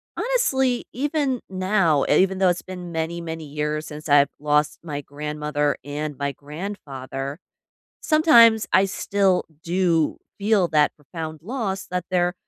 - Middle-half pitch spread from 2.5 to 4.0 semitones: No, average, 4.7 semitones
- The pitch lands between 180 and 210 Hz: No, medium, 170 Hz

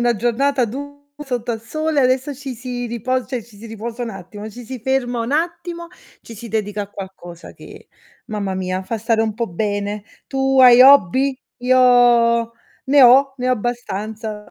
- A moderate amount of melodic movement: Yes, average, 3.4 semitones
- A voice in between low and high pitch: No, high, 240 Hz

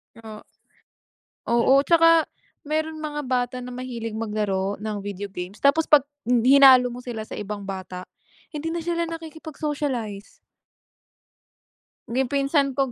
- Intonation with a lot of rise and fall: Yes, wide, 5.8 semitones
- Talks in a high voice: Yes, very high, 255 Hz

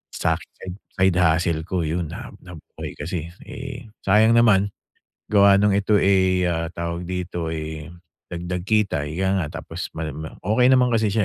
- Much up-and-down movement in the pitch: No, average, 3.4 semitones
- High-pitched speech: No, very low, 90 Hz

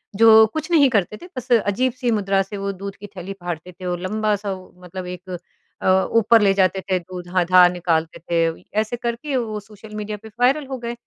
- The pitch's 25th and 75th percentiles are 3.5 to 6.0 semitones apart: Yes, average, 3.8 semitones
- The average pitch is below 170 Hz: No, high, 200 Hz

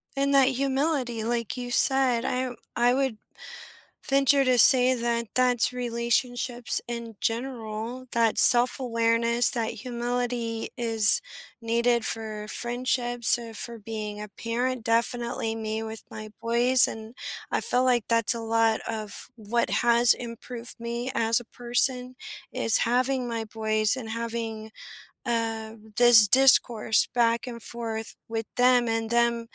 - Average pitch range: No, narrow, 1.6 semitones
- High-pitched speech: Yes, high, 235 Hz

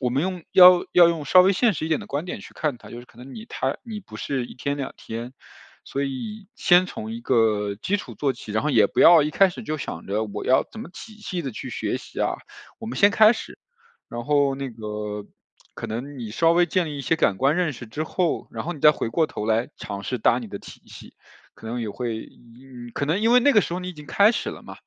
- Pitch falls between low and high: Yes, medium, 145 Hz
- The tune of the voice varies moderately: No, wide, 7.4 semitones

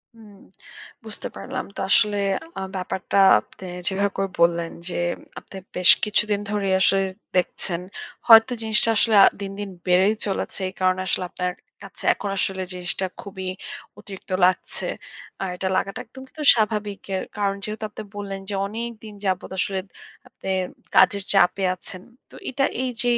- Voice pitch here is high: Yes, high, 200 Hz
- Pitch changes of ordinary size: No, narrow, 2.3 semitones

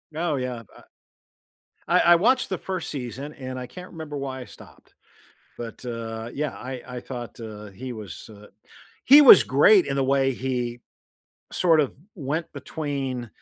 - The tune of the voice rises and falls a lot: No, average, 4.2 semitones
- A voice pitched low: Yes, low, 130 Hz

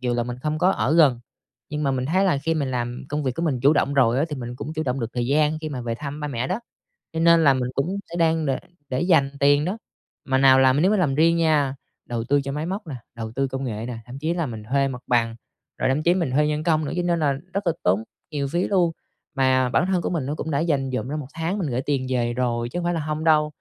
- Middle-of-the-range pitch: Yes, medium, 145 Hz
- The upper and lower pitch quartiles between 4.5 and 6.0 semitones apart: No, average, 3.9 semitones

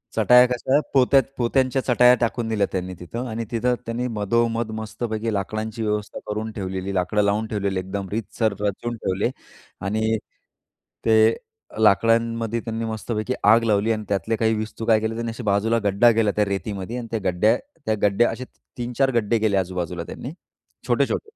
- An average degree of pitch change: No, narrow, 2.3 semitones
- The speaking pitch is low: Yes, low, 110 Hz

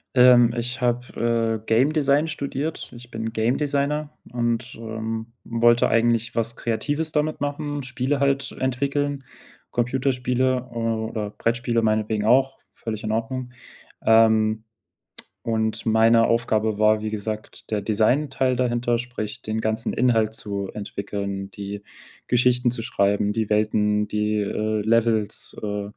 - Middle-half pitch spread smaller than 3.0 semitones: Yes, narrow, 2.6 semitones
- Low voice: Yes, low, 115 Hz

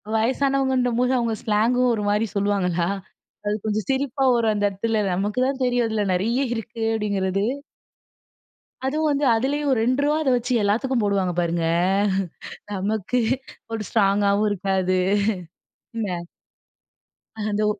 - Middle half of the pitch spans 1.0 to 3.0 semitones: No, average, 3.9 semitones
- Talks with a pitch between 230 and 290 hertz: No, high, 220 Hz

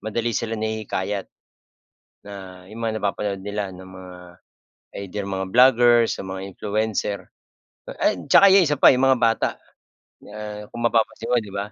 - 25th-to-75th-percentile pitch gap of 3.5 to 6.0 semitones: No, average, 3.0 semitones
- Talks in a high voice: No, low, 105 Hz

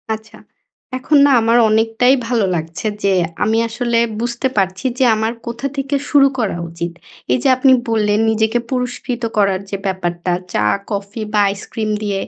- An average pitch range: Yes, average, 3.4 semitones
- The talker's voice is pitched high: Yes, high, 220 Hz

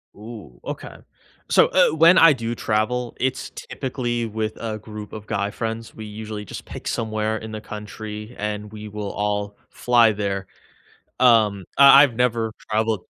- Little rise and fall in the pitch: Yes, narrow, 2.1 semitones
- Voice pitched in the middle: No, low, 110 Hz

